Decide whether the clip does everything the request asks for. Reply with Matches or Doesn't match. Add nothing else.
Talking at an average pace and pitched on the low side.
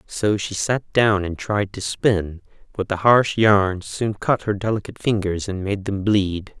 Matches